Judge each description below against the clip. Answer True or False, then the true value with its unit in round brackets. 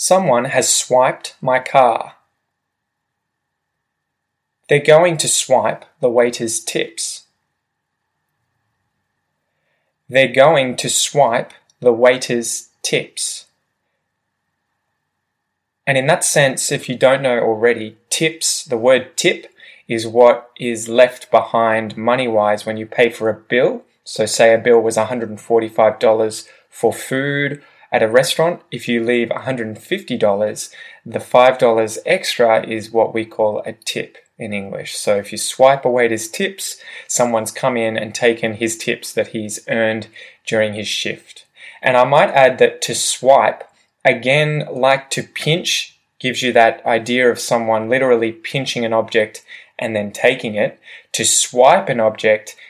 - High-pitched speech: False (120 Hz)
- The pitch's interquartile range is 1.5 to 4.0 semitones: True (2.9 semitones)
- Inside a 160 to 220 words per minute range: False (135 wpm)